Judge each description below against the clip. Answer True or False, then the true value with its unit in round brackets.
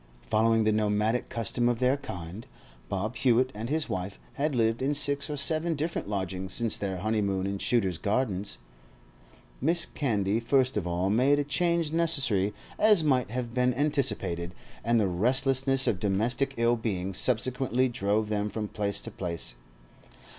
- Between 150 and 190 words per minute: True (160 wpm)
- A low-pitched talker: True (115 Hz)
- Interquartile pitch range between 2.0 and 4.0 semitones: False (4.9 semitones)